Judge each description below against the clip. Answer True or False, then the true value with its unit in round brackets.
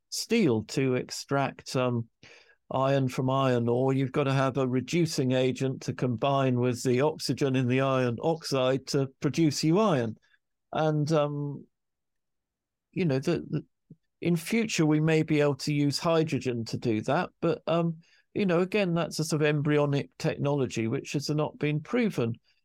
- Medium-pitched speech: True (145 Hz)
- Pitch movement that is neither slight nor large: True (3.3 semitones)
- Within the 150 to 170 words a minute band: True (160 wpm)